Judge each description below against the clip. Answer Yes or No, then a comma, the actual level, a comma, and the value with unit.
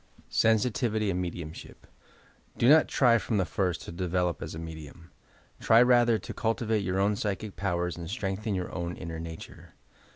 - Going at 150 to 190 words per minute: Yes, average, 165 wpm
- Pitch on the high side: No, very low, 95 Hz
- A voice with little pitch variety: No, average, 4.3 semitones